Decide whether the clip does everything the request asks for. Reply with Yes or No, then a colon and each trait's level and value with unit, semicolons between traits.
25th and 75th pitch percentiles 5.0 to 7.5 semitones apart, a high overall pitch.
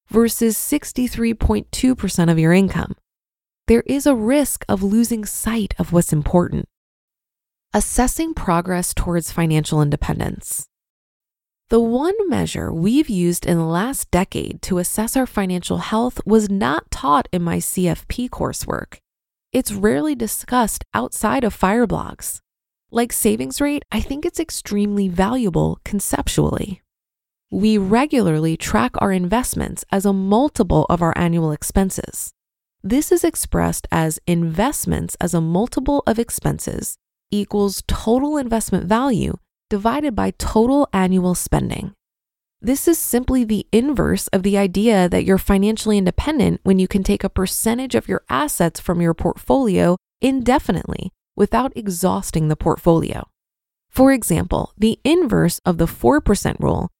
Yes: wide, 5.5 semitones; high, 210 Hz